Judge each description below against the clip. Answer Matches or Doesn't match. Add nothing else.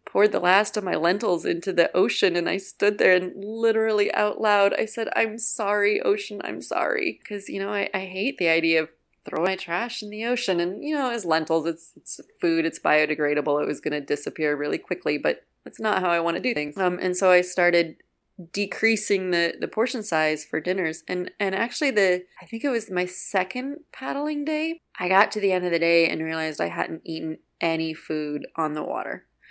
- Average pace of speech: Doesn't match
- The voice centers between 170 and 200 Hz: Matches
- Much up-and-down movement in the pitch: Doesn't match